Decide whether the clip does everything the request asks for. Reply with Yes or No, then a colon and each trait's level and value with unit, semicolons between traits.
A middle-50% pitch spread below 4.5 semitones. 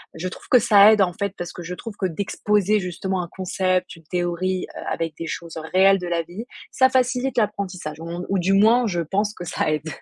Yes: average, 3.0 semitones